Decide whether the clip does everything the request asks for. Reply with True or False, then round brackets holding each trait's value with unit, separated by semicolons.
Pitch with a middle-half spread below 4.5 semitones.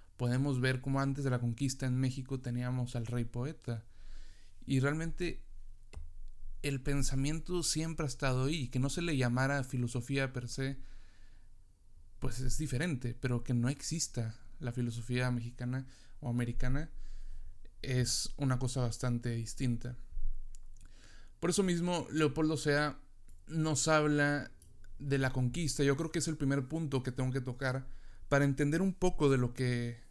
True (3.0 semitones)